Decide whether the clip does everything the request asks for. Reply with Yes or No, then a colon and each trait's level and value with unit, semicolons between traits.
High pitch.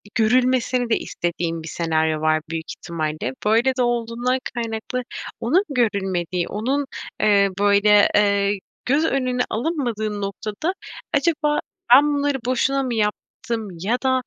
Yes: high, 225 Hz